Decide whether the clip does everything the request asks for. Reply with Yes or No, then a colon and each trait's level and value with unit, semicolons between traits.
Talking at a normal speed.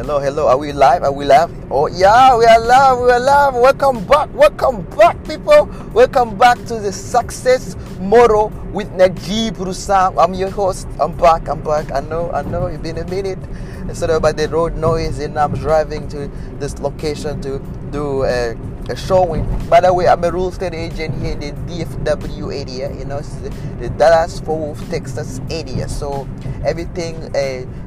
Yes: average, 185 wpm